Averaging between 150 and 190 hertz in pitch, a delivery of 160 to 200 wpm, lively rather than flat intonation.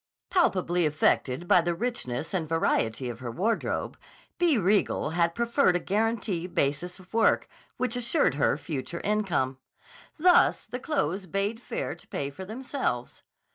No: medium, 185 Hz; average, 145 wpm; wide, 6.8 semitones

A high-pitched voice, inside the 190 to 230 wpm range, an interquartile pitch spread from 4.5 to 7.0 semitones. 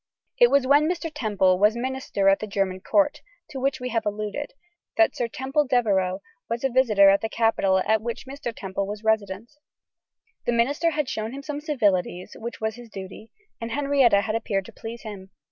Yes: high, 230 Hz; average, 195 wpm; average, 4.9 semitones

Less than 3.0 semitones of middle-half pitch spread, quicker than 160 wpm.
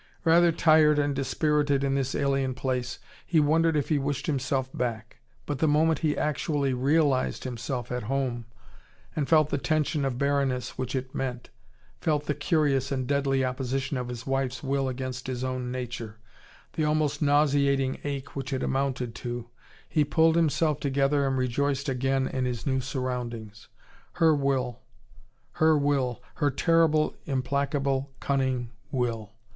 No: narrow, 2.4 semitones; average, 150 wpm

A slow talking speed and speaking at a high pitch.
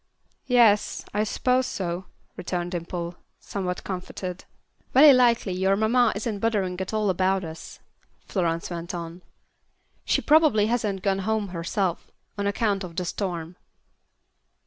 Yes: slow, 130 wpm; high, 195 Hz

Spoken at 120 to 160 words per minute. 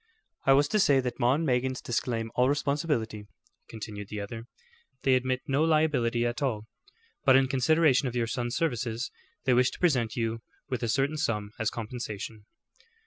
No: average, 175 wpm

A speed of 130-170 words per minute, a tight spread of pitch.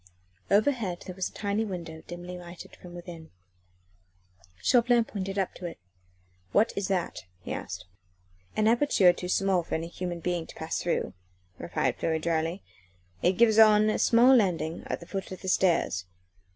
No: average, 165 wpm; average, 3.5 semitones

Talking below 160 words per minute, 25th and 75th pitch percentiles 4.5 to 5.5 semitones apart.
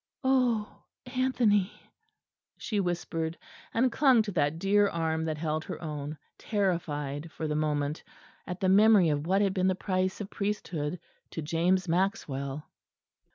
Yes: average, 145 wpm; average, 4.8 semitones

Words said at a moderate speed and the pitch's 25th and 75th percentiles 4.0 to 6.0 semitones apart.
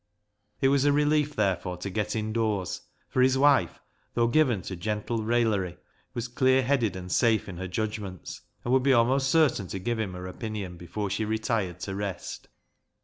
Yes: average, 180 wpm; average, 5.0 semitones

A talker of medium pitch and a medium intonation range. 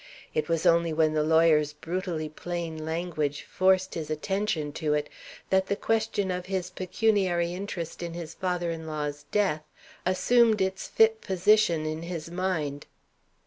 Yes: medium, 170 Hz; average, 3.4 semitones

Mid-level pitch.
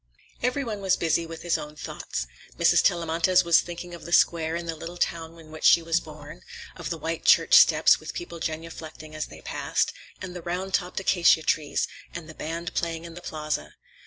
Yes: medium, 165 Hz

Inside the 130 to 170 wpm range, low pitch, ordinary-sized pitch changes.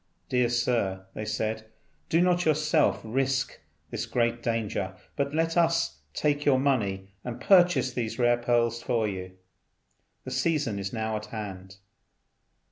Yes: average, 140 wpm; low, 120 Hz; average, 4.7 semitones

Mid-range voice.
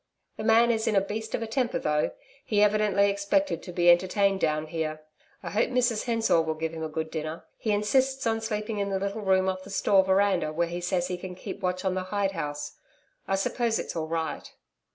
No: high, 195 Hz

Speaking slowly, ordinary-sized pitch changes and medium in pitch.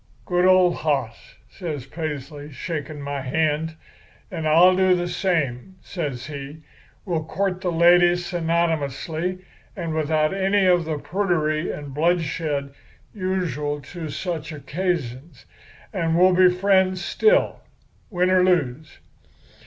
Yes: slow, 120 wpm; average, 3.5 semitones; medium, 165 Hz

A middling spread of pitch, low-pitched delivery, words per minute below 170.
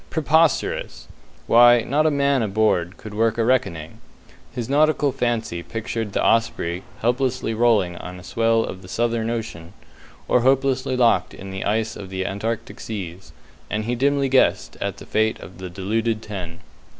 Yes: average, 4.3 semitones; low, 115 Hz; average, 160 wpm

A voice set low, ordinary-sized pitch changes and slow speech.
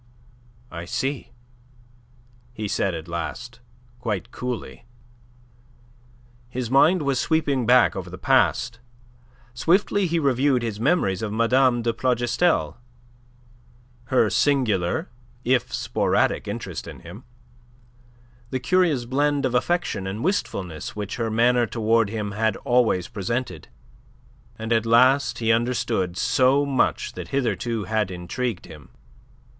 Yes: low, 120 Hz; average, 3.8 semitones; slow, 120 wpm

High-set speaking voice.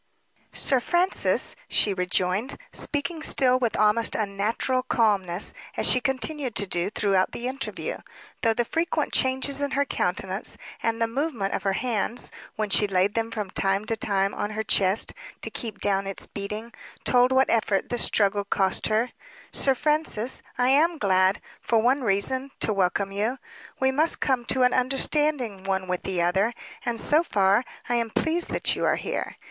Yes: high, 225 Hz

